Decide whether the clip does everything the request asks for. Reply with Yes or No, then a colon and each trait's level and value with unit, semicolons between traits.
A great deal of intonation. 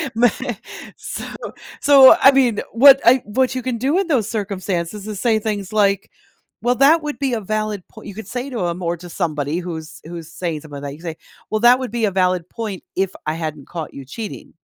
Yes: wide, 5.9 semitones